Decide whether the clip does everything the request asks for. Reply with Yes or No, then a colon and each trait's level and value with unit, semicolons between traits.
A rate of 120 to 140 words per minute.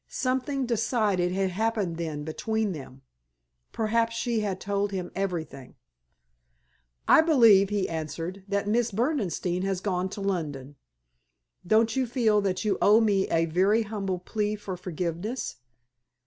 Yes: slow, 135 wpm